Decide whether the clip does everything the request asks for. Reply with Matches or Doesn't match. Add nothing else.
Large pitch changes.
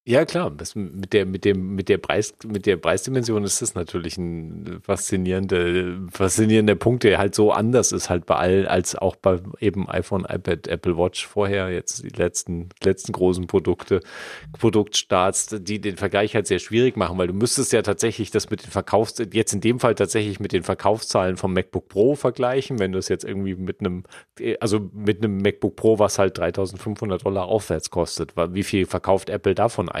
Doesn't match